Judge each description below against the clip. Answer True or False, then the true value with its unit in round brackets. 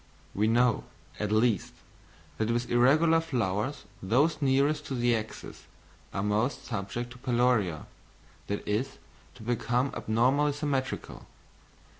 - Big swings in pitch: False (3.9 semitones)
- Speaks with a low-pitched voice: True (120 Hz)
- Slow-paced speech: True (120 wpm)